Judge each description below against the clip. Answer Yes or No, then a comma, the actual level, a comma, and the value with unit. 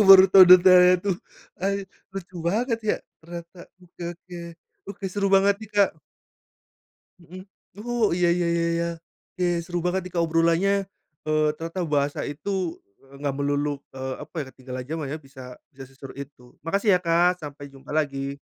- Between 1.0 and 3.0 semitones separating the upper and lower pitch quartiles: No, average, 4.7 semitones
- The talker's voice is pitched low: No, medium, 170 Hz